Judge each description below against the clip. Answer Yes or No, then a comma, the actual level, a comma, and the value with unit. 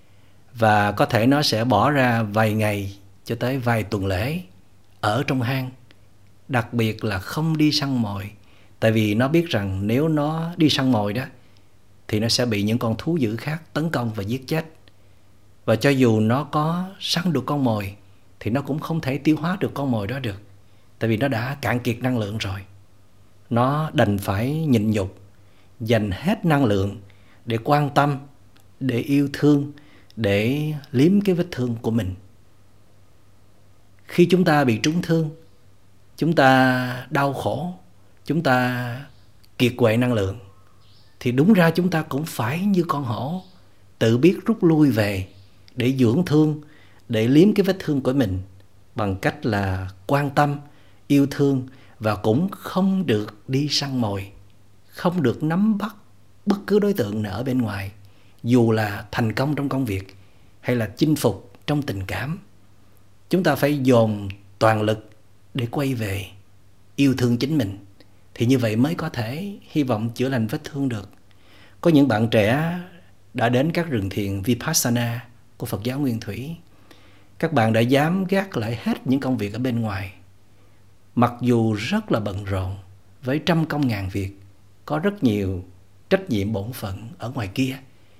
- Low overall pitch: Yes, low, 115 Hz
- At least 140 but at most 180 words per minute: Yes, average, 175 wpm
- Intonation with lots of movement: Yes, wide, 5.7 semitones